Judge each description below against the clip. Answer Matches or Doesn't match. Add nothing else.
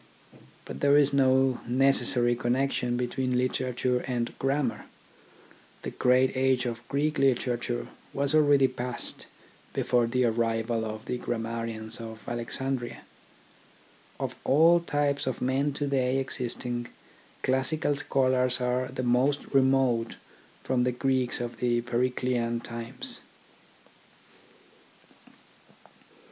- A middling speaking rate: Doesn't match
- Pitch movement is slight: Matches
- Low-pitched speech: Matches